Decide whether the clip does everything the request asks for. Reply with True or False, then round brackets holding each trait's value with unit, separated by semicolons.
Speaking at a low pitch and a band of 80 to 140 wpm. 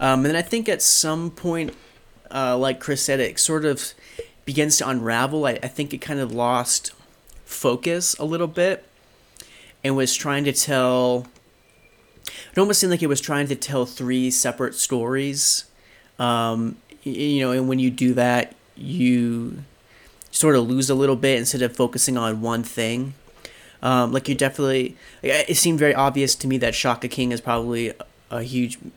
False (130 Hz; 175 wpm)